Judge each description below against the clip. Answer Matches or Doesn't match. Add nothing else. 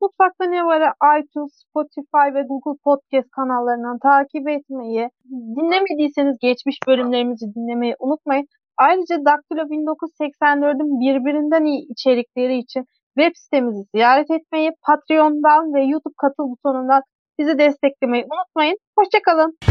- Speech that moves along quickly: Doesn't match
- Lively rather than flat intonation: Doesn't match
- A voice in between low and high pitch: Doesn't match